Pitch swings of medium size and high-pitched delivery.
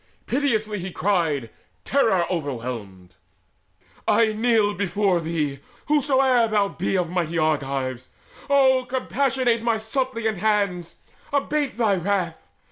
No: wide, 6.5 semitones; high, 205 Hz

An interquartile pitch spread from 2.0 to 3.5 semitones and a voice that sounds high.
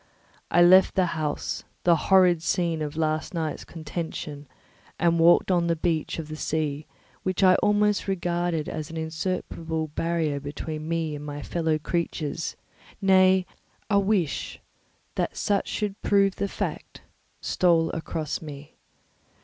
No: average, 2.9 semitones; medium, 165 Hz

